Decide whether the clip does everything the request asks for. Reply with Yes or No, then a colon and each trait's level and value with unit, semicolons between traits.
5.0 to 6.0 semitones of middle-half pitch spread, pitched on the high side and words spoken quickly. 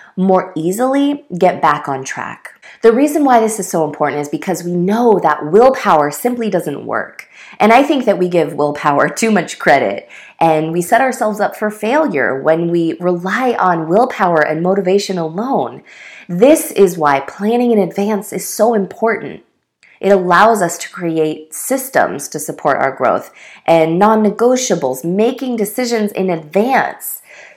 No: average, 5.3 semitones; high, 195 Hz; average, 160 wpm